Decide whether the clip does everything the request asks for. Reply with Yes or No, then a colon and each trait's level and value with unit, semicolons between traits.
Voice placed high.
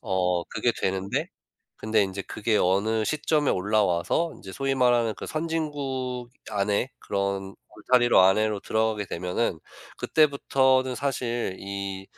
No: low, 110 Hz